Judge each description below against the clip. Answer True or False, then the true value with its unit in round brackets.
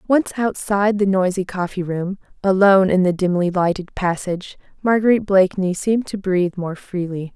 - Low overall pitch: False (190 Hz)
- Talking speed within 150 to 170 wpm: True (155 wpm)